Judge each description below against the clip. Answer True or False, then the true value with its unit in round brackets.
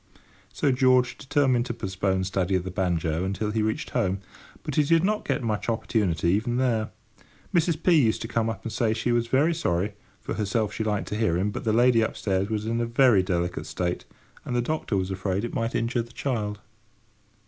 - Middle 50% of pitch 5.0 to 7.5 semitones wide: False (4.2 semitones)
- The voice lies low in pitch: True (110 Hz)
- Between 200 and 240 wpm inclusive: True (205 wpm)